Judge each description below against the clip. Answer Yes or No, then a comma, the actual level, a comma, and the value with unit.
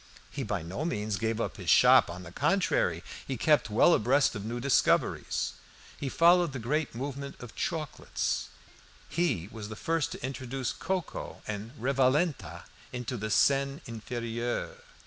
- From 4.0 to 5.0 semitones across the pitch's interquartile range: Yes, average, 4.5 semitones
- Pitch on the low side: Yes, low, 125 Hz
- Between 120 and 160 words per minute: Yes, average, 150 wpm